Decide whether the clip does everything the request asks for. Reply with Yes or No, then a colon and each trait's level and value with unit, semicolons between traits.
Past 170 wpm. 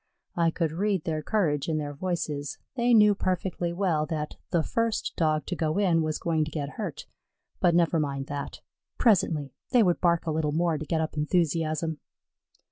Yes: average, 185 wpm